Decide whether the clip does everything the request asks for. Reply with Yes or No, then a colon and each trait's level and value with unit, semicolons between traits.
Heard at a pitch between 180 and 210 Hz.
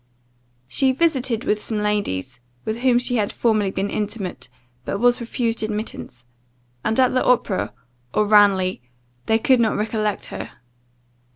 No: high, 220 Hz